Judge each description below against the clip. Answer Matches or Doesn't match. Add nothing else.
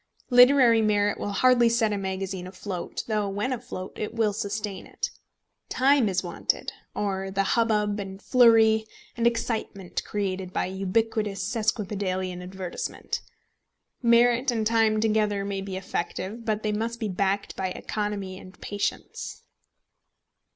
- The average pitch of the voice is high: Matches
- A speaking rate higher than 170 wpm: Doesn't match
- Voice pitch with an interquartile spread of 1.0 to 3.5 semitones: Matches